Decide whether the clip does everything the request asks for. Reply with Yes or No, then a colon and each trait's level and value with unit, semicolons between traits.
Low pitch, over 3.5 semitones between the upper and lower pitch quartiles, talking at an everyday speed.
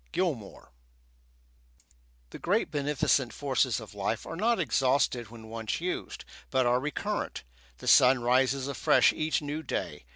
Yes: low, 130 Hz; average, 4.2 semitones; average, 150 wpm